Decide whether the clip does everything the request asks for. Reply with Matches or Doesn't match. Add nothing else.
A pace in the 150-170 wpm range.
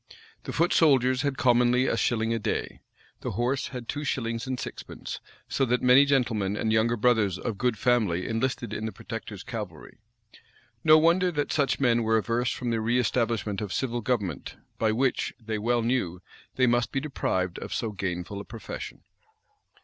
Doesn't match